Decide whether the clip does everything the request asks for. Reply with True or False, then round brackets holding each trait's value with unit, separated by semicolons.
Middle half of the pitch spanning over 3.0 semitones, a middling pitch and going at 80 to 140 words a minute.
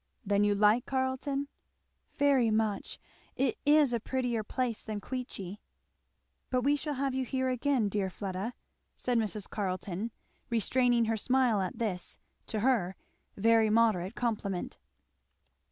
False (4.0 semitones; 230 Hz; 135 wpm)